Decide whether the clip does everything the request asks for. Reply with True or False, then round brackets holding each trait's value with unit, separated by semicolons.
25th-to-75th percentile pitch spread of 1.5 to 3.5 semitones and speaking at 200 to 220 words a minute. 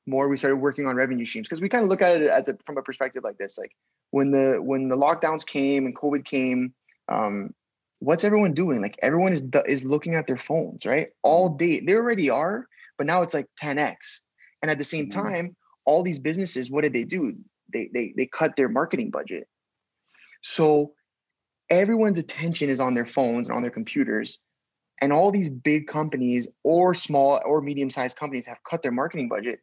False (4.2 semitones; 205 wpm)